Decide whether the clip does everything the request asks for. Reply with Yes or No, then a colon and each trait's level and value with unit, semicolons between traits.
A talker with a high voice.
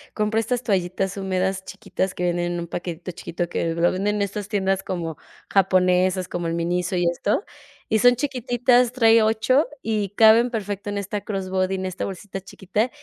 Yes: high, 195 Hz